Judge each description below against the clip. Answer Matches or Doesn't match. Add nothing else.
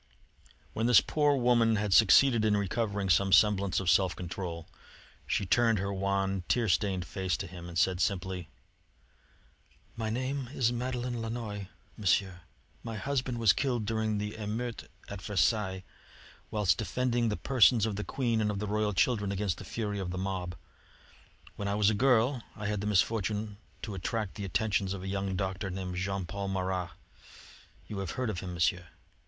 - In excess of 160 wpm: Matches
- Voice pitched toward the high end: Doesn't match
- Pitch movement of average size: Matches